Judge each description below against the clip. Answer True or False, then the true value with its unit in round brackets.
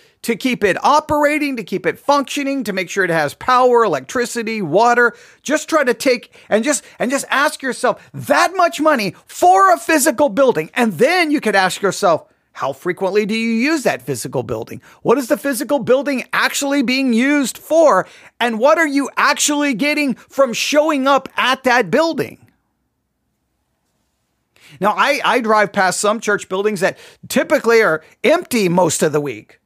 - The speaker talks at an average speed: True (170 wpm)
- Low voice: False (255 Hz)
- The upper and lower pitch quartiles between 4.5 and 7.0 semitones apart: True (5.4 semitones)